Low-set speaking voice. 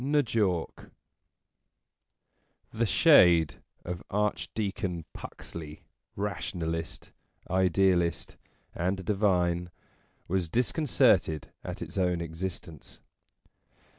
Yes: very low, 90 Hz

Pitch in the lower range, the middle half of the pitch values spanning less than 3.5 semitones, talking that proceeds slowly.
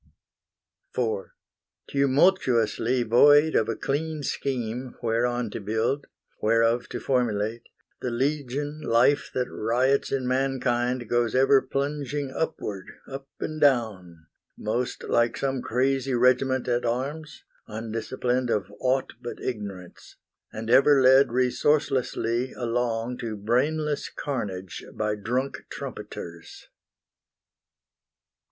Yes: low, 125 Hz; average, 3.0 semitones; slow, 105 wpm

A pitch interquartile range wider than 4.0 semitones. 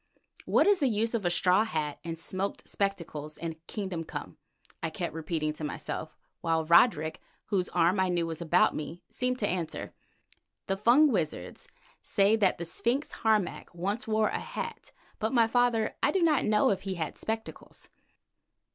Yes: average, 5.2 semitones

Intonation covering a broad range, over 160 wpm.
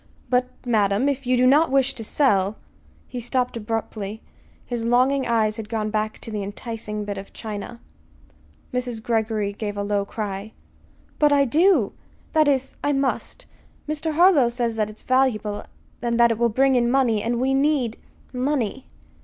No: average, 3.8 semitones; average, 175 wpm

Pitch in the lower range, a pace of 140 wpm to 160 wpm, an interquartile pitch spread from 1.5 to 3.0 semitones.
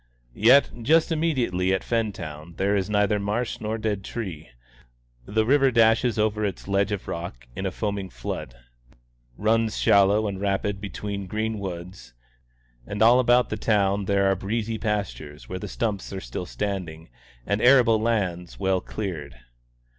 Yes: low, 100 Hz; average, 155 wpm; average, 2.7 semitones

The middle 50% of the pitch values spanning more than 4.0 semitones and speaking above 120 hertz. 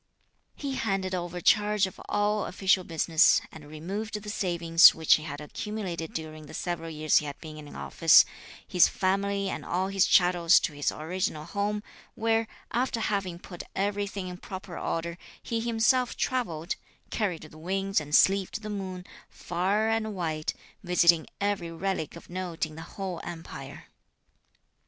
No: average, 3.6 semitones; medium, 185 Hz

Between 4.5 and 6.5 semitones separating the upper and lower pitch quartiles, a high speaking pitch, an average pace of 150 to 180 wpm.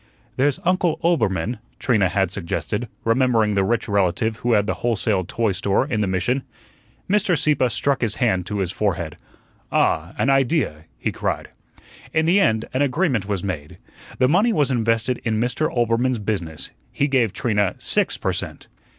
No: average, 5.2 semitones; low, 115 Hz; average, 170 wpm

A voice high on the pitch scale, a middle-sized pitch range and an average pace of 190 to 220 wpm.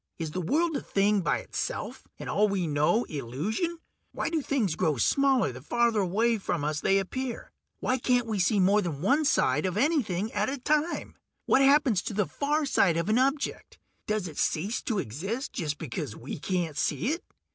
No: high, 205 Hz; wide, 7.7 semitones; average, 195 wpm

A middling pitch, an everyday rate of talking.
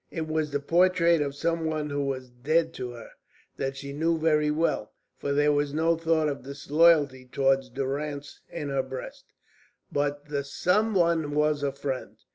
Yes: medium, 145 Hz; average, 175 wpm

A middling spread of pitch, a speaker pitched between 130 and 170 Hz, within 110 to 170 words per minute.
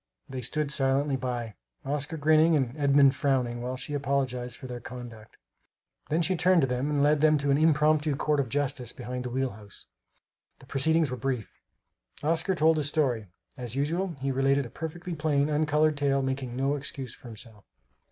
No: average, 3.1 semitones; medium, 140 Hz; average, 180 wpm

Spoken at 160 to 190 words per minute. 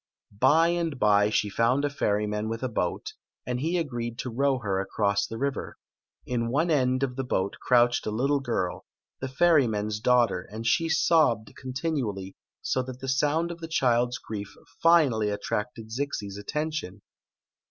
Yes: average, 165 wpm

